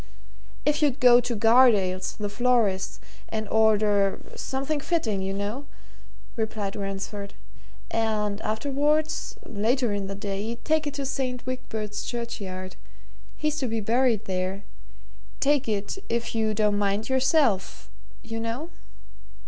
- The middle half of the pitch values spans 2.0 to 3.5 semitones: No, average, 4.2 semitones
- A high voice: Yes, high, 225 Hz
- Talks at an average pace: No, slow, 125 wpm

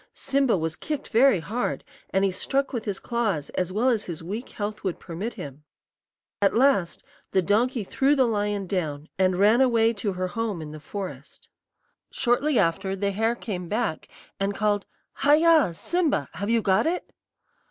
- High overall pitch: Yes, high, 205 Hz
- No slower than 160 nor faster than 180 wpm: Yes, average, 175 wpm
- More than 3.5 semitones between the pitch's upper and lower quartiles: Yes, average, 4.6 semitones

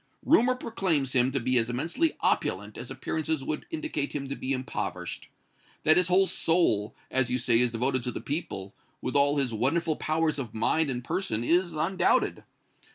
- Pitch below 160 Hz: Yes, medium, 140 Hz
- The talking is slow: No, average, 180 wpm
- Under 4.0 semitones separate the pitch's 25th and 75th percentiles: No, average, 5.1 semitones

